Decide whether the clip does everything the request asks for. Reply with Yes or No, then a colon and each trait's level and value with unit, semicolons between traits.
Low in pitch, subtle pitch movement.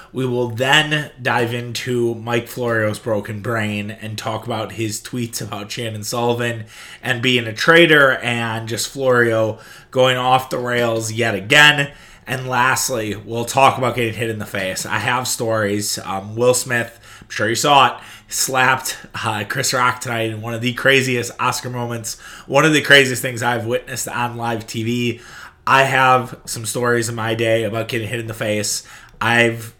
Yes: low, 120 Hz; narrow, 2.1 semitones